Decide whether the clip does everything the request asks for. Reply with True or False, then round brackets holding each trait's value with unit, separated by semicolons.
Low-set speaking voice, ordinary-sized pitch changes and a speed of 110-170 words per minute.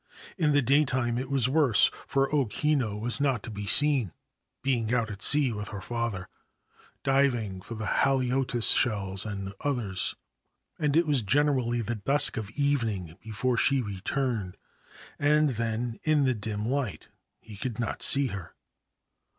True (120 Hz; 4.7 semitones; 155 wpm)